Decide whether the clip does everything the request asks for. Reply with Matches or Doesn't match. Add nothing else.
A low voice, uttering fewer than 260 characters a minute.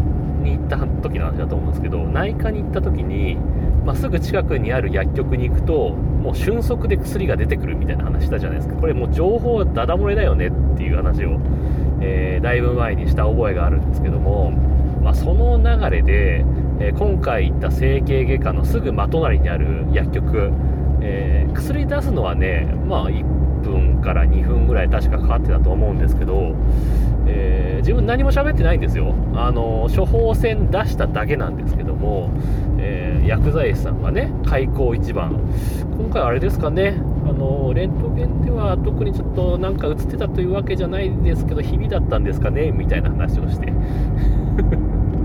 Doesn't match